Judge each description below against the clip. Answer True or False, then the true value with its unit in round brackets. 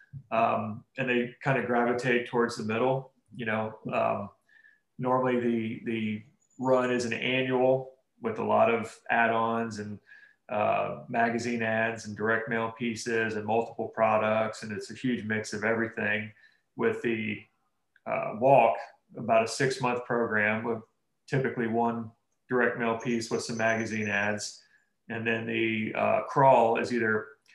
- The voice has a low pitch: True (115 Hz)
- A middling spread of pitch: False (1.8 semitones)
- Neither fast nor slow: True (150 wpm)